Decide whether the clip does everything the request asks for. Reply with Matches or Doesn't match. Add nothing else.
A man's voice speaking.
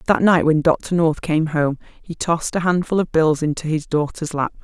Doesn't match